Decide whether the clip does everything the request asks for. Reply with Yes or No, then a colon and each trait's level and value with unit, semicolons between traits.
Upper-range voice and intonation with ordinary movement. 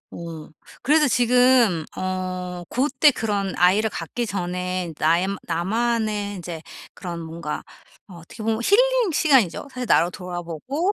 No: high, 195 Hz; wide, 5.9 semitones